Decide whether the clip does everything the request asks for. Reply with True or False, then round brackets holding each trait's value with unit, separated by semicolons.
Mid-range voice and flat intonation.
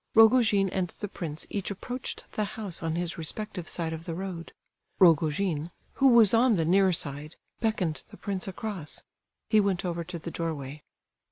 False (180 Hz; 4.1 semitones)